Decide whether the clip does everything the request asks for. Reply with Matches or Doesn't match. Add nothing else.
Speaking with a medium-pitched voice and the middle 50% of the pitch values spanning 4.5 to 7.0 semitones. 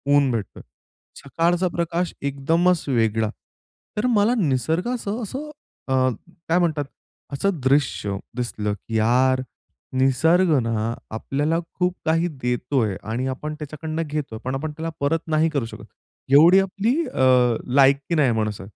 Matches